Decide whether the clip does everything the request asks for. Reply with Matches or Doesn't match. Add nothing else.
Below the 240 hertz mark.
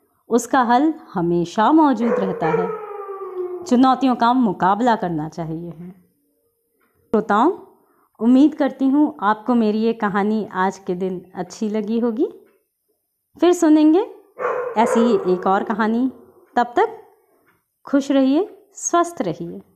Doesn't match